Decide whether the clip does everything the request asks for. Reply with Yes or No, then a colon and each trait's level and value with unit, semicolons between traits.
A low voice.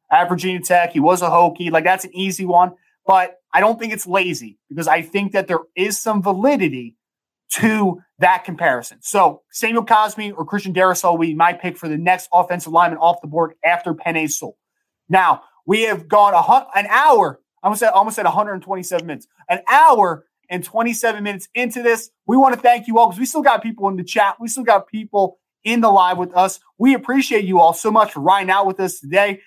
No: high, 190 Hz